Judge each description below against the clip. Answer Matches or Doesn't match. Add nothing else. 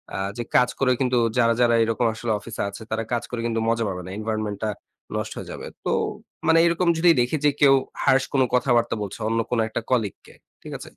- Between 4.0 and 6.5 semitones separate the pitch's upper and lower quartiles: Doesn't match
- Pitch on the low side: Matches